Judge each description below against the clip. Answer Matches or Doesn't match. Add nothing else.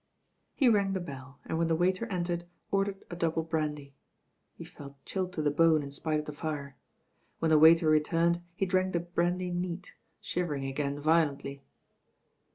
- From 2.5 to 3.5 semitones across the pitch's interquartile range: Matches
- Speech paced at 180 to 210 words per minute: Doesn't match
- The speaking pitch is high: Doesn't match